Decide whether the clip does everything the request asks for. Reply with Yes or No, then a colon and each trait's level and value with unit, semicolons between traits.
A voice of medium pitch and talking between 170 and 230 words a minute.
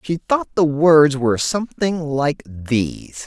No: medium, 150 Hz; average, 145 wpm